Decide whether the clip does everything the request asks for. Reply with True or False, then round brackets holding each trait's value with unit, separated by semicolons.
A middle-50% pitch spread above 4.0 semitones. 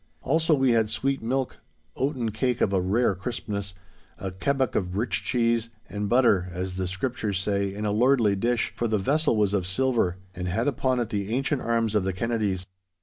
True (4.4 semitones)